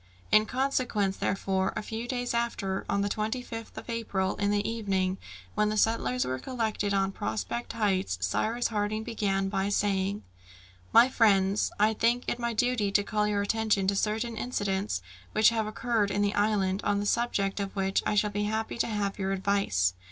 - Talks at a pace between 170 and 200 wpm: Yes, average, 185 wpm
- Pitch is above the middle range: Yes, high, 205 Hz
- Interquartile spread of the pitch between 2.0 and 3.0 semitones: Yes, narrow, 2.5 semitones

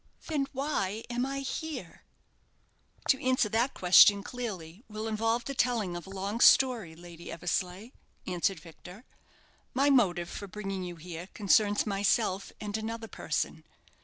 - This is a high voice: Yes, high, 210 Hz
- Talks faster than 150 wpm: No, average, 140 wpm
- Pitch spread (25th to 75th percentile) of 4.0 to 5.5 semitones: Yes, average, 5.1 semitones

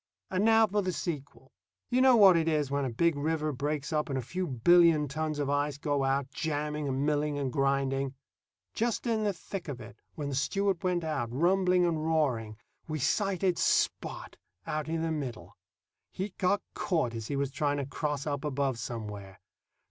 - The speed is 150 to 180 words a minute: No, average, 190 wpm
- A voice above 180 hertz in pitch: No, medium, 150 Hz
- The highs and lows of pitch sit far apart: No, average, 4.0 semitones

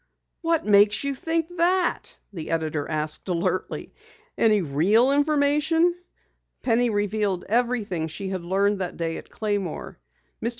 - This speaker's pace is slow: Yes, slow, 130 wpm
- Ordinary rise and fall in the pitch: No, wide, 7.9 semitones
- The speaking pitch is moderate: No, high, 205 Hz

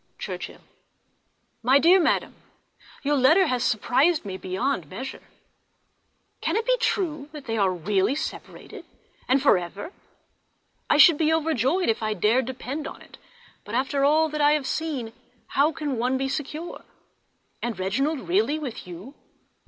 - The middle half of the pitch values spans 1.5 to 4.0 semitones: No, average, 5.3 semitones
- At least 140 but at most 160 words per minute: Yes, average, 150 wpm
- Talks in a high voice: Yes, very high, 275 Hz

